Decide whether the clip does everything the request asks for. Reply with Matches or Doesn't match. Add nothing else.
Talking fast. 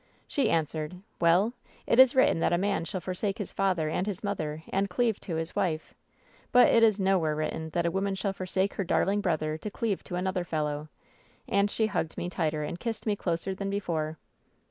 Matches